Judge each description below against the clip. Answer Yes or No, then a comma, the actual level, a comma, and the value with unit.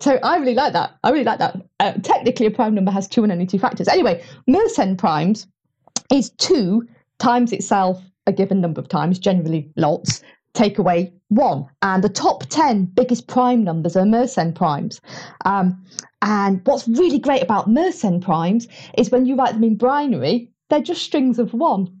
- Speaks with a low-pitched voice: No, high, 210 Hz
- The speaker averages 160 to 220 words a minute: Yes, average, 185 wpm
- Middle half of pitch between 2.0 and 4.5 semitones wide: No, average, 4.9 semitones